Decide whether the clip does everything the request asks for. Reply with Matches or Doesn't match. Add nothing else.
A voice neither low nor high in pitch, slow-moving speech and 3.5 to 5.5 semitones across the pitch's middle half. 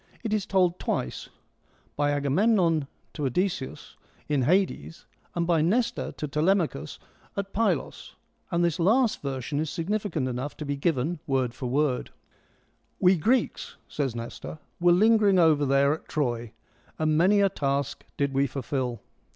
Doesn't match